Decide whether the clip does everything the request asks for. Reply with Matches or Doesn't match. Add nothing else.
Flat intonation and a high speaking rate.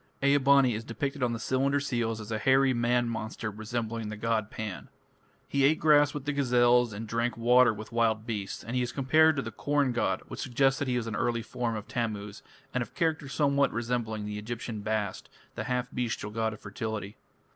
Doesn't match